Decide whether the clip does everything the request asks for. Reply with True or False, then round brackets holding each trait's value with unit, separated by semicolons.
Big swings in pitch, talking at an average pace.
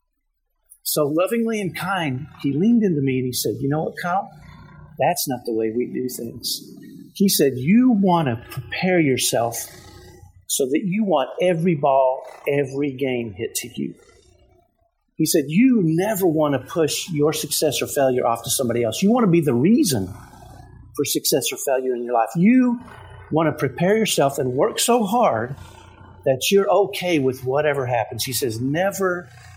True (6.9 semitones; 175 wpm)